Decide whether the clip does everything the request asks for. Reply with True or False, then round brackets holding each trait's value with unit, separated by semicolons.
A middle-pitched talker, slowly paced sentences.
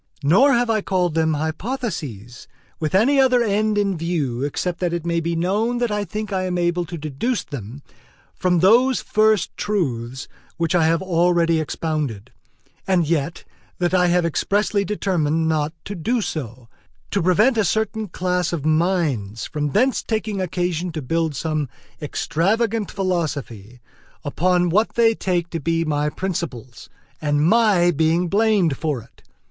False (175 Hz; 160 wpm)